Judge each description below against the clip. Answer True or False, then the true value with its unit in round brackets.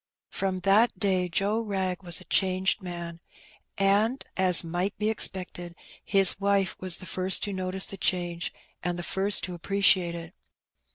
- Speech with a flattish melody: True (1.9 semitones)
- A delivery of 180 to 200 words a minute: False (165 wpm)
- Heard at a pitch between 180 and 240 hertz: True (185 Hz)